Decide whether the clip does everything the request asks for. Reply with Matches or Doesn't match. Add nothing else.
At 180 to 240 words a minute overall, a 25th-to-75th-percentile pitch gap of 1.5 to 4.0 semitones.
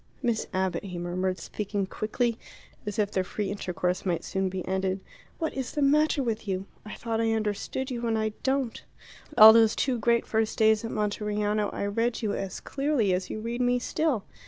Matches